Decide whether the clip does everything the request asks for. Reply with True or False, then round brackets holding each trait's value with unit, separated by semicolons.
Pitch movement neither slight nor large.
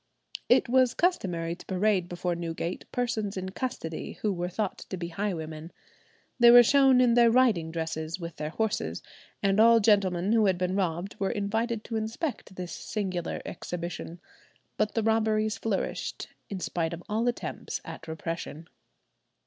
True (4.6 semitones)